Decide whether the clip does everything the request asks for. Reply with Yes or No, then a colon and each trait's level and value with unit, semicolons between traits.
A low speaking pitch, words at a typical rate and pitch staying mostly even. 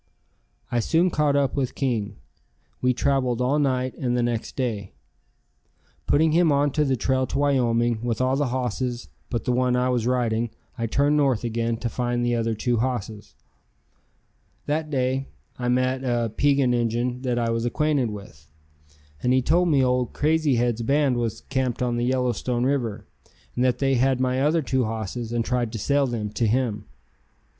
Yes: low, 125 Hz; average, 180 wpm; narrow, 2.3 semitones